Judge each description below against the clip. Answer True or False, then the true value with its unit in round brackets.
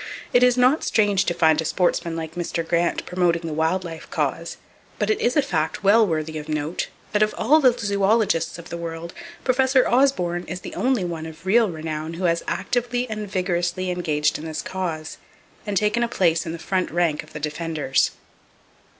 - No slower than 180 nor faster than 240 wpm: True (195 wpm)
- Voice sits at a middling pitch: True (175 Hz)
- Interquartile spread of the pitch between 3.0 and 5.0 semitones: True (4.7 semitones)